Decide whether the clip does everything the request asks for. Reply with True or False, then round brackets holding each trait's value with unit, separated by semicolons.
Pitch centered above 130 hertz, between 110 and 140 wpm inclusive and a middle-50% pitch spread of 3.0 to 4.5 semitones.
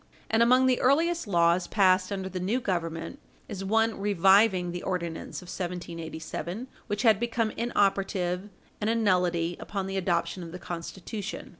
False (190 Hz; 155 wpm; 3.9 semitones)